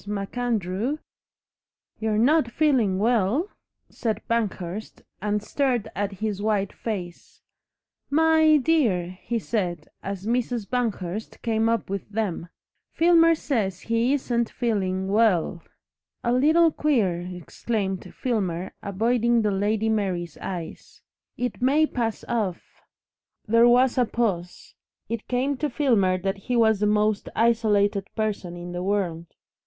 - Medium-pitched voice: No, high, 220 Hz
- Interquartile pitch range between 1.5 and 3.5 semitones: No, average, 4.1 semitones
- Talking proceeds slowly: Yes, slow, 130 wpm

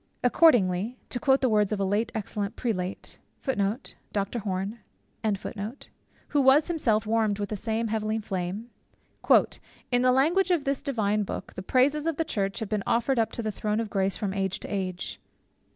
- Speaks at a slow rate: No, average, 170 wpm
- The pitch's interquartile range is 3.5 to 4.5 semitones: Yes, average, 4.2 semitones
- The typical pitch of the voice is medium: No, high, 220 Hz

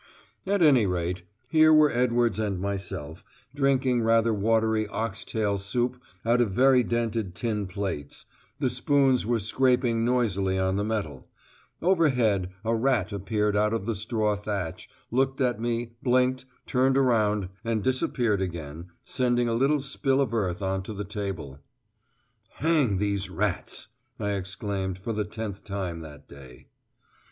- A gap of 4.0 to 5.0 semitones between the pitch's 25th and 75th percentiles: Yes, average, 4.3 semitones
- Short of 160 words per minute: Yes, average, 145 wpm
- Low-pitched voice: Yes, low, 110 Hz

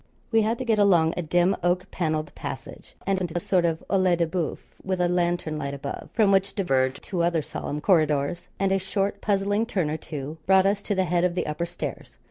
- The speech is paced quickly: Yes, fast, 225 wpm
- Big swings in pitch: No, average, 3.4 semitones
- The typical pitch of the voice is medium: Yes, medium, 175 Hz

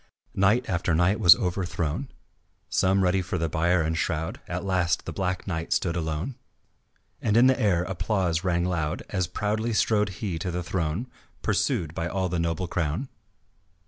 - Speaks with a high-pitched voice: No, very low, 90 Hz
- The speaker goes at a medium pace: Yes, average, 170 wpm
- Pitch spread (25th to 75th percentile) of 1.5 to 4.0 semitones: Yes, average, 2.8 semitones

